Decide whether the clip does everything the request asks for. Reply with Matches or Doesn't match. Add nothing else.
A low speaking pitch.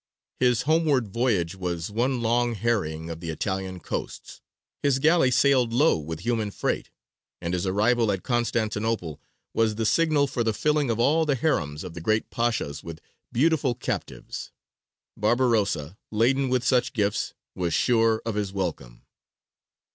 Matches